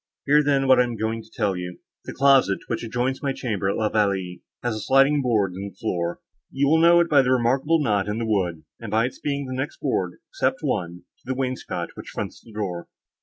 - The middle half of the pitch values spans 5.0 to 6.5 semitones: Yes, wide, 5.4 semitones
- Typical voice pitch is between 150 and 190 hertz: No, low, 115 Hz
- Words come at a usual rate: No, fast, 235 wpm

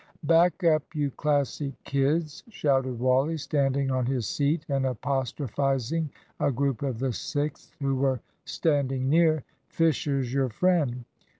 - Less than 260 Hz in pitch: Yes, medium, 140 Hz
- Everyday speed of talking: No, slow, 130 wpm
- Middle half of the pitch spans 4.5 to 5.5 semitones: No, narrow, 2.6 semitones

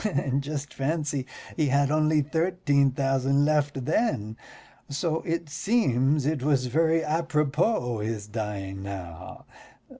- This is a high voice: No, medium, 140 Hz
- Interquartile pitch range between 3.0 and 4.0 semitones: Yes, average, 3.5 semitones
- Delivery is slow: Yes, slow, 120 wpm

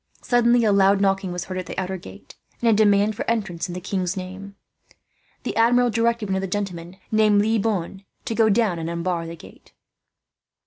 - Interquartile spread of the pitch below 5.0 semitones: Yes, average, 3.2 semitones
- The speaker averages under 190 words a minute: No, fast, 205 wpm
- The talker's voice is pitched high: Yes, high, 195 Hz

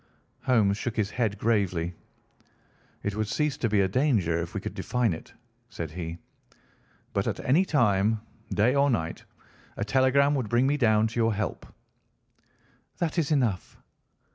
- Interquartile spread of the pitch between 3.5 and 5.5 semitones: Yes, average, 4.8 semitones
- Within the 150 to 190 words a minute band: Yes, average, 160 wpm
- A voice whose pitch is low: Yes, low, 110 Hz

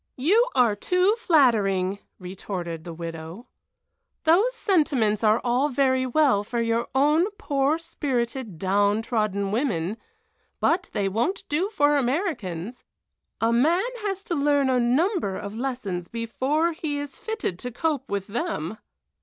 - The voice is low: No, very high, 250 Hz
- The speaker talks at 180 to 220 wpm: No, slow, 135 wpm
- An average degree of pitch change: No, wide, 7.4 semitones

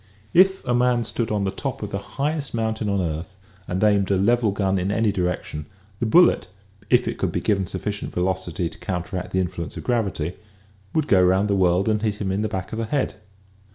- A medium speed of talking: No, fast, 220 wpm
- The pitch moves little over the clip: No, average, 3.4 semitones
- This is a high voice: No, low, 100 Hz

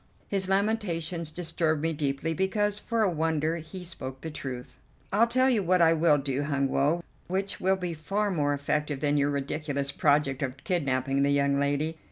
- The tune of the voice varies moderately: Yes, average, 4.4 semitones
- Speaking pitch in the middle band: Yes, medium, 155 Hz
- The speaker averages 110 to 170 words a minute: No, average, 185 wpm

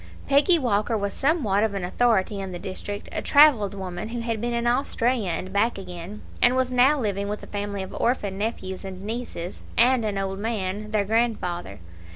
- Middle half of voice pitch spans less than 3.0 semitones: No, average, 3.7 semitones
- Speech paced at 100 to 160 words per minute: No, average, 190 wpm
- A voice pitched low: No, high, 210 Hz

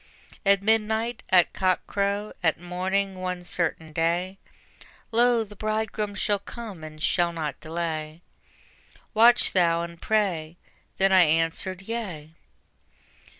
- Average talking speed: No, slow, 120 wpm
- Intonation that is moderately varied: Yes, average, 3.9 semitones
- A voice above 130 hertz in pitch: Yes, medium, 185 Hz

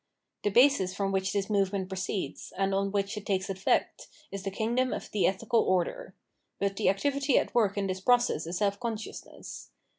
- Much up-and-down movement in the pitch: No, narrow, 2.6 semitones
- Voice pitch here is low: No, high, 200 Hz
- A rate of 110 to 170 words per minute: No, average, 185 wpm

